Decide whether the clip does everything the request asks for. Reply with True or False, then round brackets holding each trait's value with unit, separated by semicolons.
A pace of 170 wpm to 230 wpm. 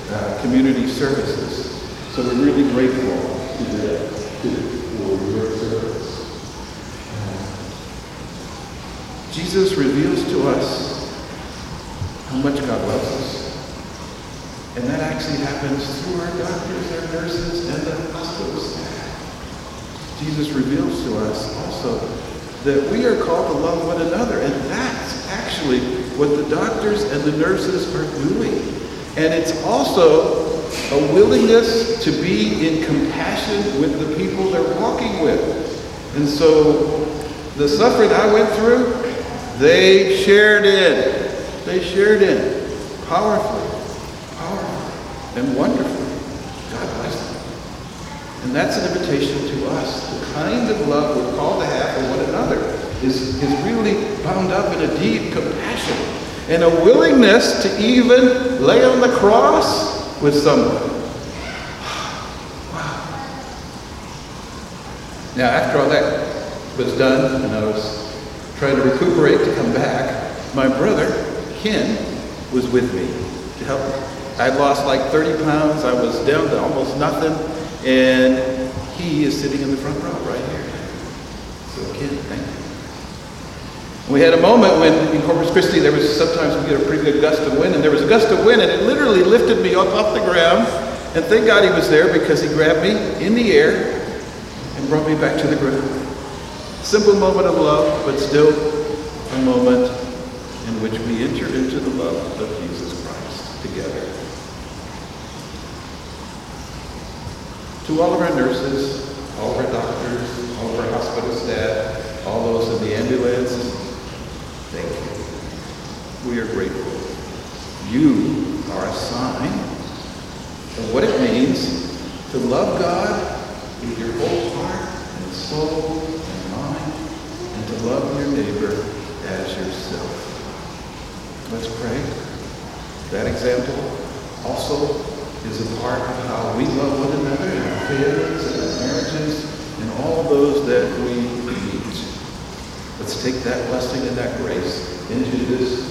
False (140 wpm)